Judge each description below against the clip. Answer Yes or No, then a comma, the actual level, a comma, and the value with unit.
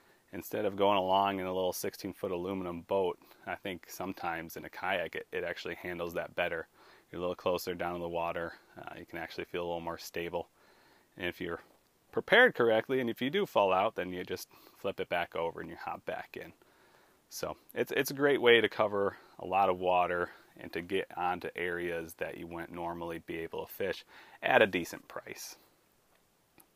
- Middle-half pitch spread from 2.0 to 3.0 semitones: Yes, narrow, 2.6 semitones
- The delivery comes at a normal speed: No, fast, 210 wpm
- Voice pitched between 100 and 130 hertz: No, very low, 90 Hz